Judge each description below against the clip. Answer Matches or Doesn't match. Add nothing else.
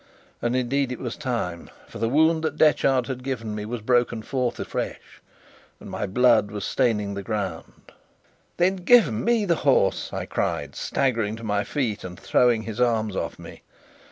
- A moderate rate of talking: Matches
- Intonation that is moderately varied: Matches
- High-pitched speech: Doesn't match